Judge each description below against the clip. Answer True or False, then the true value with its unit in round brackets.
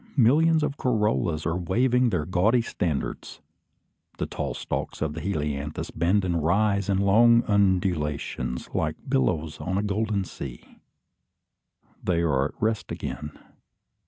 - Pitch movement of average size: False (5.7 semitones)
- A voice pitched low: True (95 Hz)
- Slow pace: True (130 wpm)